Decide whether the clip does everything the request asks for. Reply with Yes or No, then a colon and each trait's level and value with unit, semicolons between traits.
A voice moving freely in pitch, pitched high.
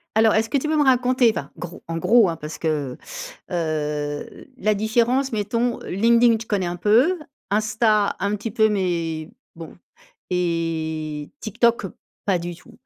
Yes: wide, 5.8 semitones; high, 205 Hz